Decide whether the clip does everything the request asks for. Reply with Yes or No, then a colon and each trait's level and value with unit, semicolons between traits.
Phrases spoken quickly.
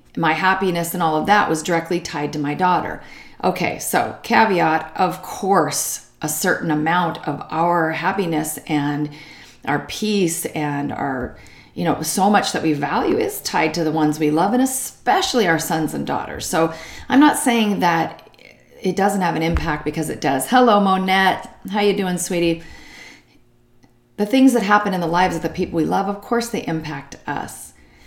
No: average, 180 wpm